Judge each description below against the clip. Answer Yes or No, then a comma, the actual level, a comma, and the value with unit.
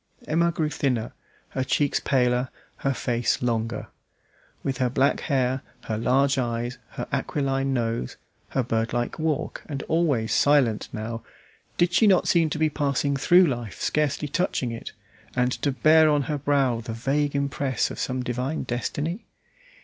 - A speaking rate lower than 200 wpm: Yes, average, 155 wpm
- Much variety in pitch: No, average, 3.5 semitones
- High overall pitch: No, low, 135 Hz